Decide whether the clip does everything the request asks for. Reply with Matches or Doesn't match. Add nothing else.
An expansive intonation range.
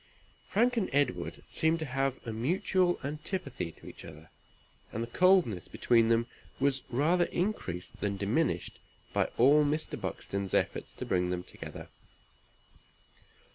Matches